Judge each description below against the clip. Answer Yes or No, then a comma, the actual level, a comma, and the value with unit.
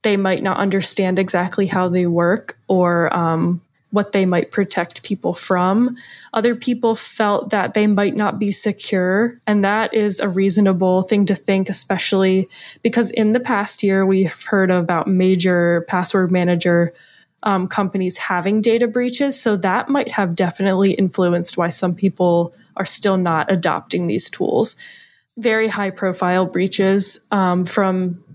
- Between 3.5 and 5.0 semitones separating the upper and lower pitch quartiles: No, narrow, 2.4 semitones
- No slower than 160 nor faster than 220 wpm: No, average, 150 wpm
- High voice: Yes, high, 195 Hz